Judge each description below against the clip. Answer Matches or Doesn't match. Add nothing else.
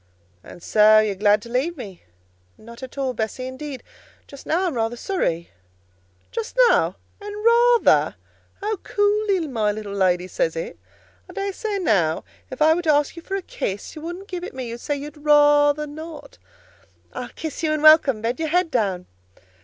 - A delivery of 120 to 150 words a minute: Doesn't match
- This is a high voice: Matches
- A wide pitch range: Matches